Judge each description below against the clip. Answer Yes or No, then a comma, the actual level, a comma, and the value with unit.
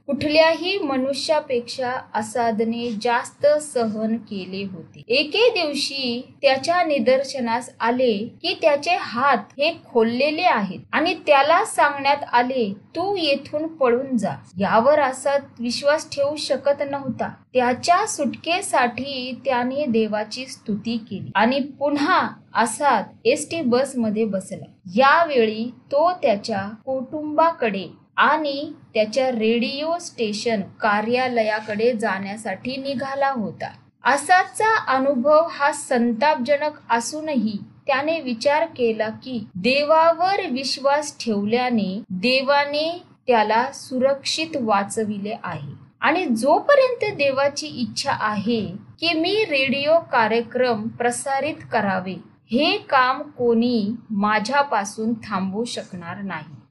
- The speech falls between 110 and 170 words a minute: No, average, 95 wpm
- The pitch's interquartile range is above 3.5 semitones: Yes, average, 4.7 semitones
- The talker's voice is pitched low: No, very high, 255 Hz